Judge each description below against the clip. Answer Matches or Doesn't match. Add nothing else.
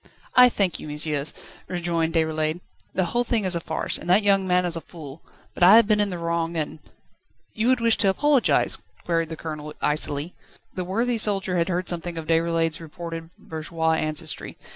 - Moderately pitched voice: Matches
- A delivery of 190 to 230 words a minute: Matches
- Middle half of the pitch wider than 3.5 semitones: Doesn't match